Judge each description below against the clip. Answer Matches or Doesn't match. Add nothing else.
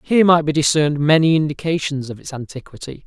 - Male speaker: Matches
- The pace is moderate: Matches